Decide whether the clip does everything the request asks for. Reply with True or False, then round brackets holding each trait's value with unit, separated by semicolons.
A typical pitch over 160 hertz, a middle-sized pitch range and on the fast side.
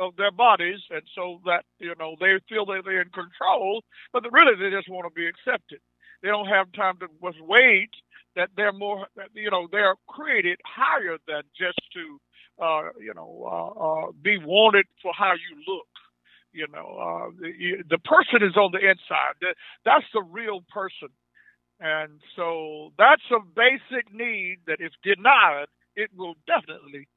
False (190 Hz; 4.0 semitones; 170 wpm)